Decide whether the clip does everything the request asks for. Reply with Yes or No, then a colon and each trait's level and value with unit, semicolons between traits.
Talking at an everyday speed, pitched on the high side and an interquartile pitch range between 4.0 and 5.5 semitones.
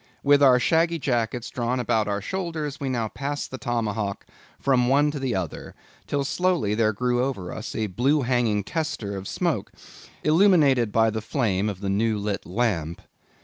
No: average, 175 wpm; low, 120 Hz; average, 5.2 semitones